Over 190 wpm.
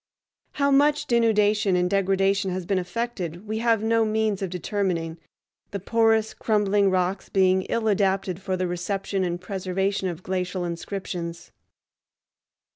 No: slow, 135 wpm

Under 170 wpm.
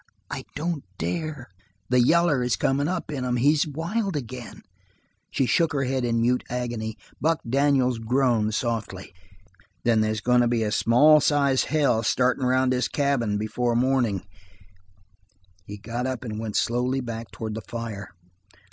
Yes: average, 155 wpm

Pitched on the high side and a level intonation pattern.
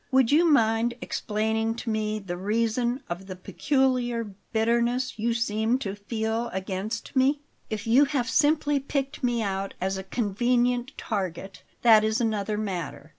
No: high, 225 Hz; average, 3.2 semitones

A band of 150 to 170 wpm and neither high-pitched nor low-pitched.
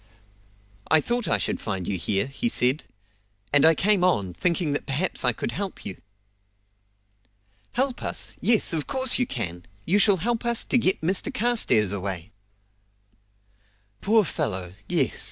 Yes: average, 155 wpm; medium, 165 Hz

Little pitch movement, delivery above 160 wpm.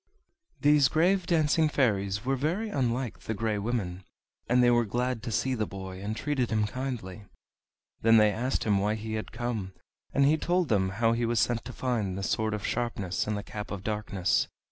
No: average, 3.8 semitones; average, 200 wpm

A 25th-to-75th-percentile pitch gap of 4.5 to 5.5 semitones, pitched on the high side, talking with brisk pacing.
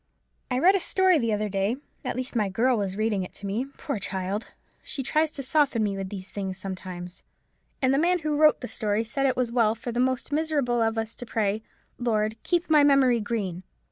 Yes: average, 5.1 semitones; high, 230 Hz; fast, 210 wpm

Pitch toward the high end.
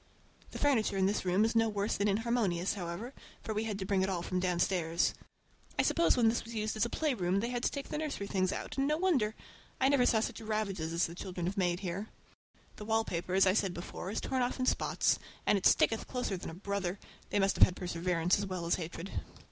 Yes: high, 200 Hz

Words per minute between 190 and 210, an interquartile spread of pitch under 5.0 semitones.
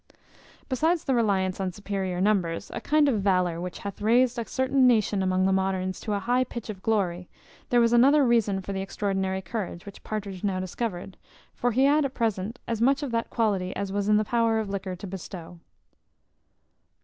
Yes: average, 195 wpm; average, 3.8 semitones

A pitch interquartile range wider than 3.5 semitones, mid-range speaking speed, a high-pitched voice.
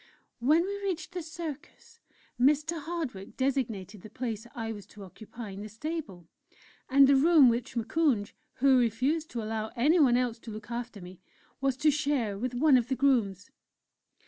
Yes: wide, 5.4 semitones; average, 170 wpm; very high, 250 Hz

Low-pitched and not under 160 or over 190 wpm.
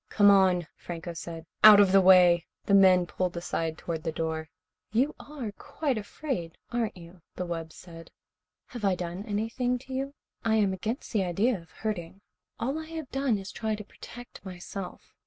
No: high, 195 Hz; average, 180 wpm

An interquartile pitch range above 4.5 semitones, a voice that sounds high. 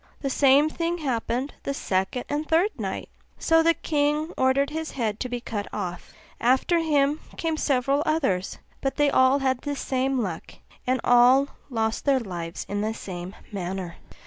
Yes: average, 4.9 semitones; very high, 265 Hz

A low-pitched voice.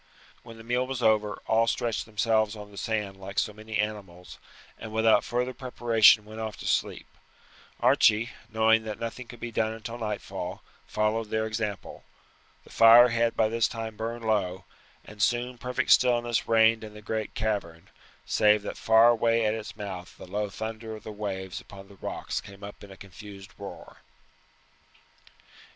Yes: low, 110 Hz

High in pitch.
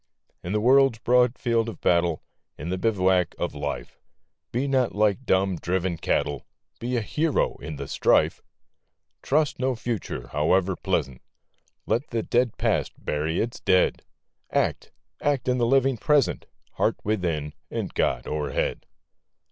No: low, 105 Hz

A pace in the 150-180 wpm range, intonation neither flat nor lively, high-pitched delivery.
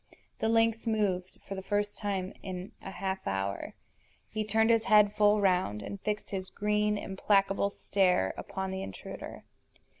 No: average, 155 wpm; narrow, 1.9 semitones; high, 200 Hz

